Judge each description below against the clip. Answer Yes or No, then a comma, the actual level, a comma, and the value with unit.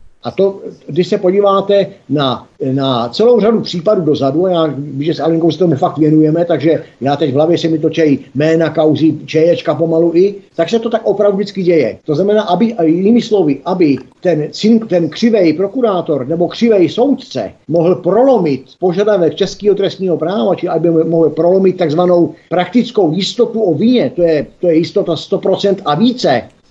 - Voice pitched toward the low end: No, medium, 175 Hz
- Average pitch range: Yes, average, 3.9 semitones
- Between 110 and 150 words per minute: No, fast, 170 wpm